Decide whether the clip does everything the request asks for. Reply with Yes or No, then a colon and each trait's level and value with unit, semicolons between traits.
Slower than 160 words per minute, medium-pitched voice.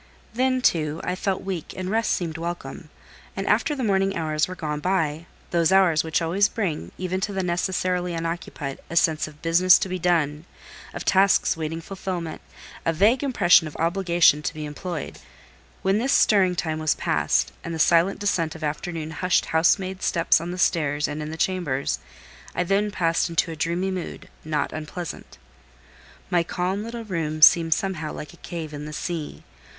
No: average, 175 wpm; medium, 170 Hz